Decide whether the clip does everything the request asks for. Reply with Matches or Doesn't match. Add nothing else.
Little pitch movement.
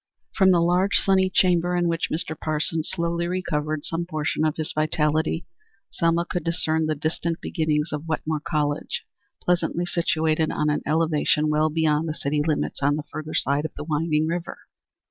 Matches